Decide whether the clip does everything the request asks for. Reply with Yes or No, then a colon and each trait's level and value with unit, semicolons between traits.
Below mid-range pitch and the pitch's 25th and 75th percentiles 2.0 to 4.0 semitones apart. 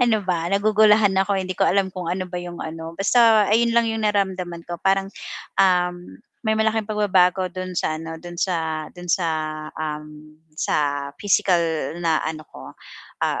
No: medium, 180 Hz; average, 3.7 semitones